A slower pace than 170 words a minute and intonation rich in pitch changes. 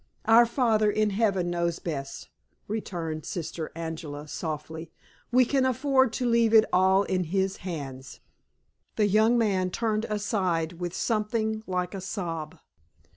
No: slow, 135 wpm; average, 4.8 semitones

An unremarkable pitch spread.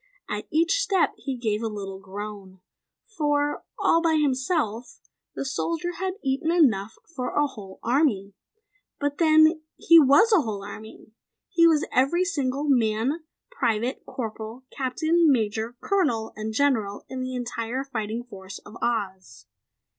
No: wide, 6.3 semitones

